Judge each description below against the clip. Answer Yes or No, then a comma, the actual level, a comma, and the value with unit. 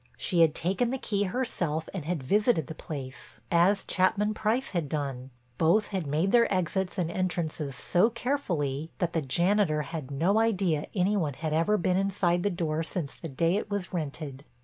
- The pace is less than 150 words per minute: No, average, 185 wpm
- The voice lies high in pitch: No, medium, 175 Hz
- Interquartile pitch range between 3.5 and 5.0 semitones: Yes, average, 4.6 semitones